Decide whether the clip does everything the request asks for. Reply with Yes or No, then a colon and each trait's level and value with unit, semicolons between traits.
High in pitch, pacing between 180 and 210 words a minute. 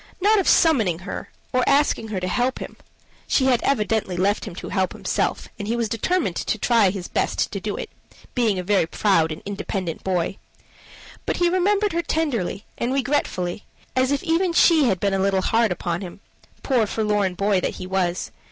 Yes: high, 210 Hz; average, 200 wpm